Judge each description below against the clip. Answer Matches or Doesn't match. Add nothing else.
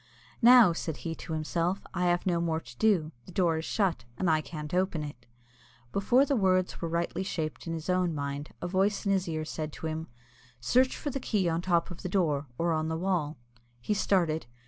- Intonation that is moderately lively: Matches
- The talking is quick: Matches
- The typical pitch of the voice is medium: Matches